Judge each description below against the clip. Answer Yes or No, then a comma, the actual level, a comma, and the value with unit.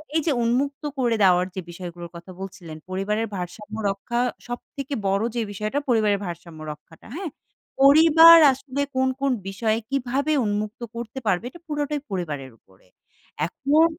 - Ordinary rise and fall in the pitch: No, wide, 6.9 semitones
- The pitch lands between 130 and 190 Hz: No, high, 215 Hz